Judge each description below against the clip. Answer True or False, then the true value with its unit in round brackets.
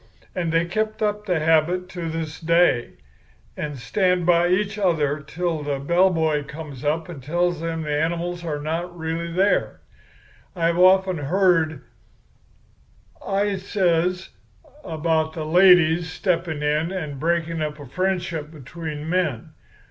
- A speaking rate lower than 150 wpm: True (135 wpm)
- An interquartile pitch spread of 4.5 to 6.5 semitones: False (2.6 semitones)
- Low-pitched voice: False (165 Hz)